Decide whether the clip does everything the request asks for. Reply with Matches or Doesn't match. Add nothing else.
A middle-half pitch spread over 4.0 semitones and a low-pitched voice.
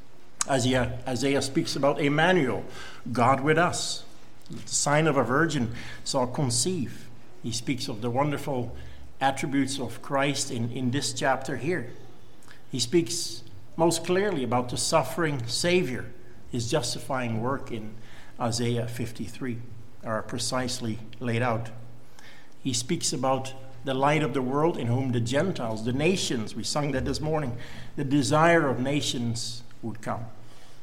Doesn't match